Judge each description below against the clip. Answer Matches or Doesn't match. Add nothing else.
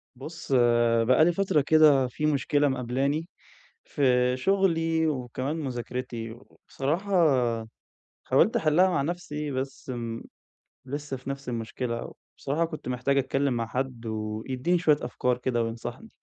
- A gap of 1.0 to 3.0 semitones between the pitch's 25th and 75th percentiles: Doesn't match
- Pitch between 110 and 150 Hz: Matches